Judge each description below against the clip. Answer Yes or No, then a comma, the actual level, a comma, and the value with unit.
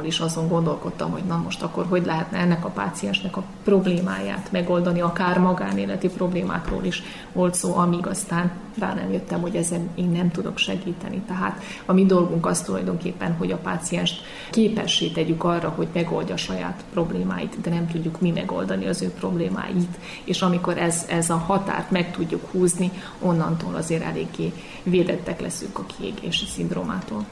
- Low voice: No, medium, 175 Hz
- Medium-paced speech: No, fast, 165 wpm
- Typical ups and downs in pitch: No, narrow, 1.8 semitones